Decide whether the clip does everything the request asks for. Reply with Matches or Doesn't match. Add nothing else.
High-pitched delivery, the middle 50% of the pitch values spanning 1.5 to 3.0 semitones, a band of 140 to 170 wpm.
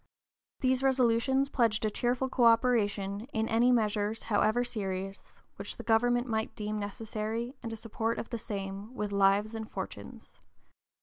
Matches